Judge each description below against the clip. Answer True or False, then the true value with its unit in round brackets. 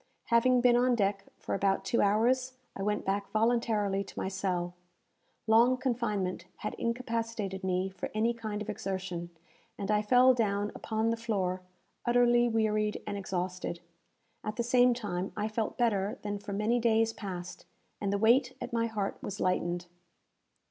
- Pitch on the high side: True (215 Hz)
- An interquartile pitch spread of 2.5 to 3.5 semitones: True (3.1 semitones)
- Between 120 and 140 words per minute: False (160 wpm)